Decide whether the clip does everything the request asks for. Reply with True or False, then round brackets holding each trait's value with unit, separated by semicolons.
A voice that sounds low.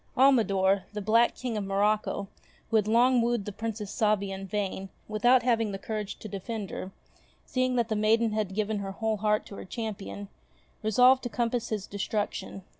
False (215 Hz)